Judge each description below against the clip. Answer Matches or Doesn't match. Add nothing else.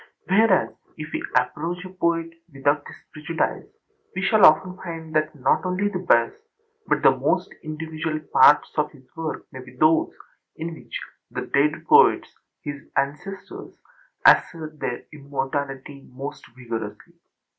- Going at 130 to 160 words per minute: Matches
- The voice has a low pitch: Doesn't match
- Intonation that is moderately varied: Matches